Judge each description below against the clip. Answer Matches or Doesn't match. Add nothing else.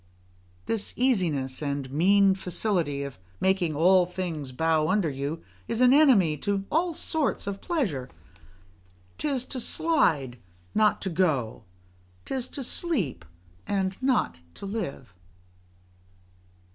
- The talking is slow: Matches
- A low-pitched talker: Doesn't match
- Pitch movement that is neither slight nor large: Doesn't match